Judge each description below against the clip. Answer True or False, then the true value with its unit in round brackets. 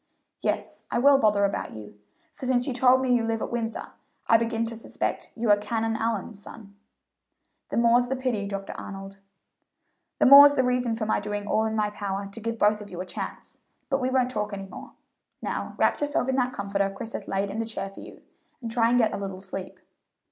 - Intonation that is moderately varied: True (3.4 semitones)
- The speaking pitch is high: True (225 Hz)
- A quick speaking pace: True (220 wpm)